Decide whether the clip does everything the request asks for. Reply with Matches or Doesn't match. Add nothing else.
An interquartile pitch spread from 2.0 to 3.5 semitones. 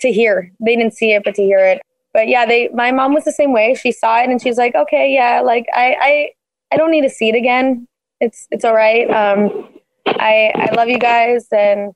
Matches